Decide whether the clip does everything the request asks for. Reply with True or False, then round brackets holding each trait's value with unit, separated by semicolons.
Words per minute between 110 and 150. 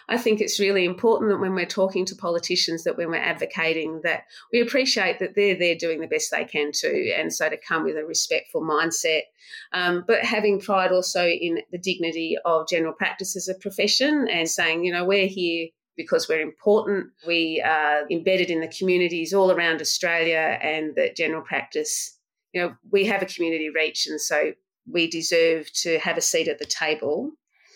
False (190 wpm)